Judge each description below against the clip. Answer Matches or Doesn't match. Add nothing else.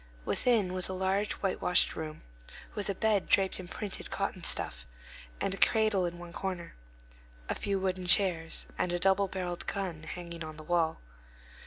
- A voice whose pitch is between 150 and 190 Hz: Matches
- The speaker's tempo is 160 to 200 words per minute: Matches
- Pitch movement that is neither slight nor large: Doesn't match